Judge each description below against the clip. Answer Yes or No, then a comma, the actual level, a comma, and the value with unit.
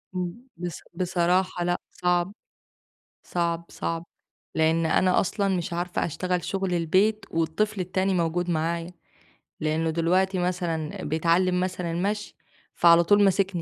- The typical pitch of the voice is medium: Yes, medium, 175 Hz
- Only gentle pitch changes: Yes, narrow, 1.9 semitones